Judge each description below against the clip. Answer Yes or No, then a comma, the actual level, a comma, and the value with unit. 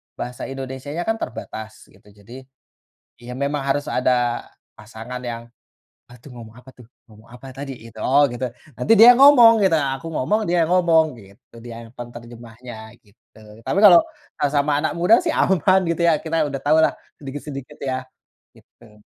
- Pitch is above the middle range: No, low, 135 Hz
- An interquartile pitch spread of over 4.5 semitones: Yes, average, 5.3 semitones